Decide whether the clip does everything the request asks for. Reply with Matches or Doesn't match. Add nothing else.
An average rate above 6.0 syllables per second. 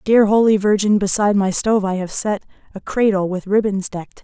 Doesn't match